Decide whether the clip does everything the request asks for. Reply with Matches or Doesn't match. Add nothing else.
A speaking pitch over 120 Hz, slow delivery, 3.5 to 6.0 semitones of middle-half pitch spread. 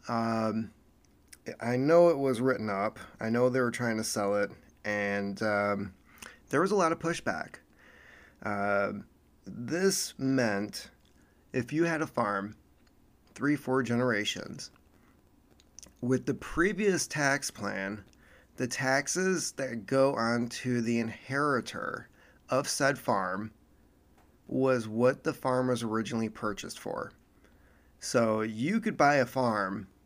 Doesn't match